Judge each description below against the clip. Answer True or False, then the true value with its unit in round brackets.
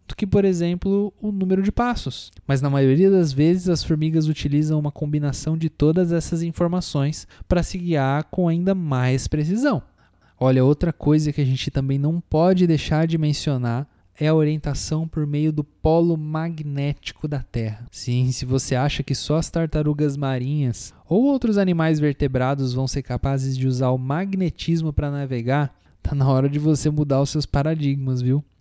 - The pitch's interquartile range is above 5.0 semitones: False (3.5 semitones)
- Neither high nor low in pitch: True (150 Hz)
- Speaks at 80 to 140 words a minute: False (170 wpm)